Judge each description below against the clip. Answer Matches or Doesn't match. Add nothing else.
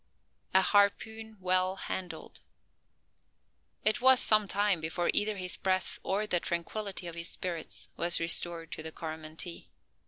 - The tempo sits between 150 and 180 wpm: Doesn't match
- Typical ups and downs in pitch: Matches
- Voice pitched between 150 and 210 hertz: Matches